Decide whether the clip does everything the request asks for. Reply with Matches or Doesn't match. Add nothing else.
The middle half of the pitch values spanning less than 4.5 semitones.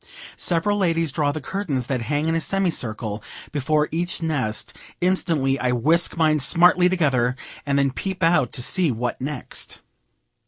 Doesn't match